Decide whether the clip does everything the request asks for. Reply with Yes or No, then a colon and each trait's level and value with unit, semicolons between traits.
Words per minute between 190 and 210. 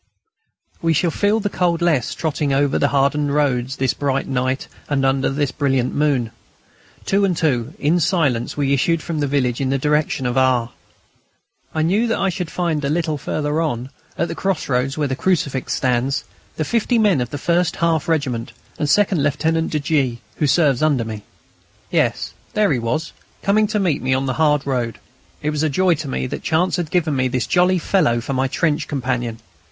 Yes: average, 200 wpm